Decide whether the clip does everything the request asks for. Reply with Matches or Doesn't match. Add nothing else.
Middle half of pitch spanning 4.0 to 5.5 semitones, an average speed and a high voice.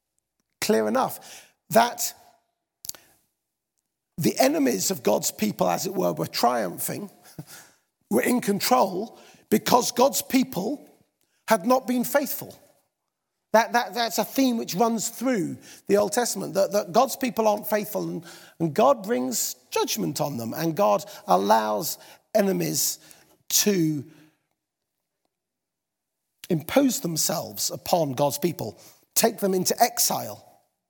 Doesn't match